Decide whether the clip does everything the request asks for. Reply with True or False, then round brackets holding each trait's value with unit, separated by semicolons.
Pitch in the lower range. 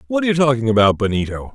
True (125 Hz)